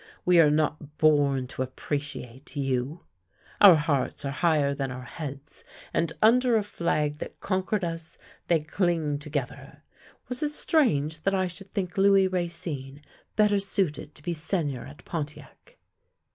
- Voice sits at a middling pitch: Yes, medium, 155 Hz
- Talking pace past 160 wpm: No, average, 145 wpm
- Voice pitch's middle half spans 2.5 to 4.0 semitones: No, average, 4.6 semitones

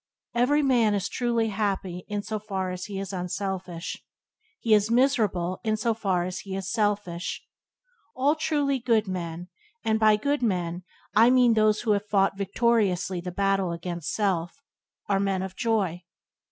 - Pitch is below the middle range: No, high, 205 Hz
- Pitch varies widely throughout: No, average, 3.6 semitones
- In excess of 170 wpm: No, average, 165 wpm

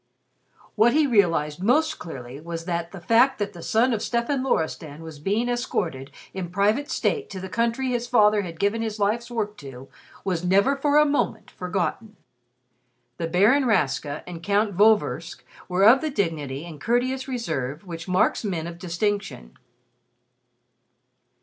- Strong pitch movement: Yes, wide, 6.0 semitones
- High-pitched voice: Yes, high, 200 Hz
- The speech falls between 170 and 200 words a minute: No, average, 155 wpm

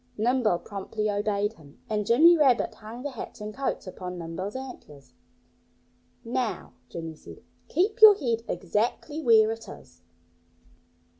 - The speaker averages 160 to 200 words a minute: No, slow, 135 wpm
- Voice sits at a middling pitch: No, high, 220 Hz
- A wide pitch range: No, average, 4.8 semitones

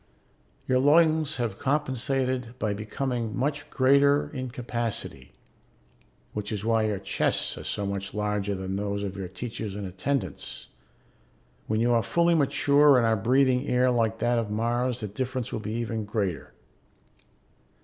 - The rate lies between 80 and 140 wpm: No, average, 150 wpm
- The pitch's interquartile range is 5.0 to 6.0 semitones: No, average, 3.9 semitones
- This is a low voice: Yes, low, 115 Hz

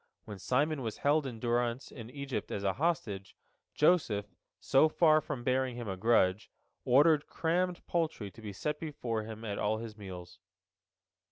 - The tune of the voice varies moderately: No, wide, 6.0 semitones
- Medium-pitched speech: No, low, 120 Hz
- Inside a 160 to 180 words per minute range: Yes, average, 165 wpm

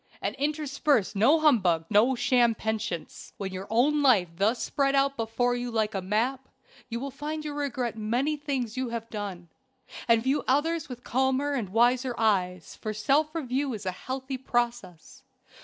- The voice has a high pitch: Yes, high, 245 Hz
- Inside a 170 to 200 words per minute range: Yes, average, 175 wpm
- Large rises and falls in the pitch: No, average, 4.3 semitones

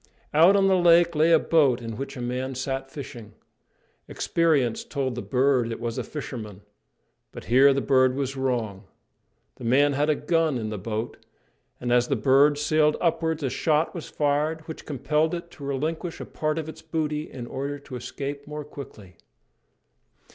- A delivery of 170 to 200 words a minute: Yes, average, 180 wpm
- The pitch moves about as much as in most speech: Yes, average, 3.8 semitones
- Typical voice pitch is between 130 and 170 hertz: Yes, medium, 140 Hz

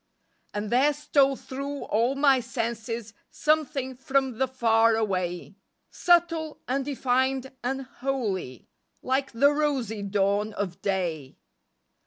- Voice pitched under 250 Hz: No, very high, 255 Hz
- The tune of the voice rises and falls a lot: No, average, 4.4 semitones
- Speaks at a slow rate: Yes, slow, 110 wpm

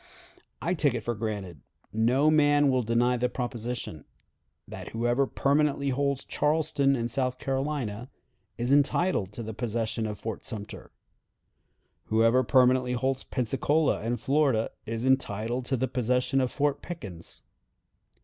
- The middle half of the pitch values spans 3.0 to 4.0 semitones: Yes, average, 3.4 semitones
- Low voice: Yes, low, 125 Hz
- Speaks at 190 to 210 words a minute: No, slow, 135 wpm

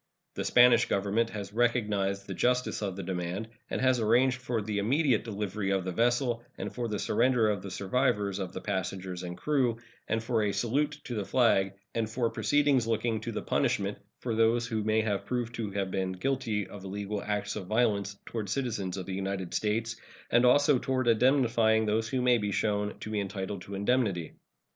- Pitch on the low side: Yes, low, 110 Hz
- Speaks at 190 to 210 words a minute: Yes, average, 195 wpm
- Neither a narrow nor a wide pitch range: Yes, average, 3.4 semitones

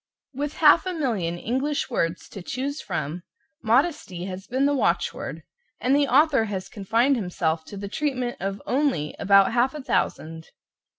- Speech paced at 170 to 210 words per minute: No, average, 160 wpm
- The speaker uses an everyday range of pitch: No, wide, 7.0 semitones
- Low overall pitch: No, high, 235 Hz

